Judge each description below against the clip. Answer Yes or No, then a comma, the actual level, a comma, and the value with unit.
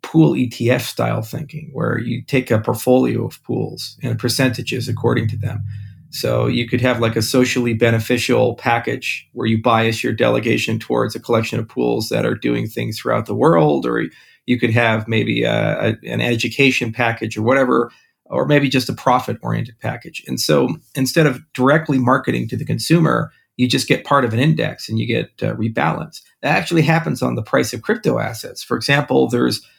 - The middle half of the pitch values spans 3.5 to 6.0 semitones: No, average, 2.8 semitones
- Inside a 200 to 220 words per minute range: No, average, 185 wpm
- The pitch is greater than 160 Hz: No, low, 120 Hz